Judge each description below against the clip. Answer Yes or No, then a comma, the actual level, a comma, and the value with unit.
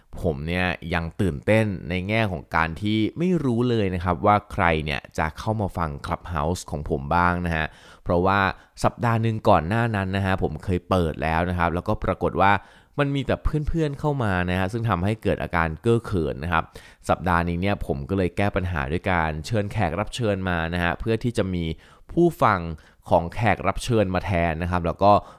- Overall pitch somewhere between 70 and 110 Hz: Yes, very low, 90 Hz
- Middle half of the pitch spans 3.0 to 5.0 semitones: Yes, average, 4.0 semitones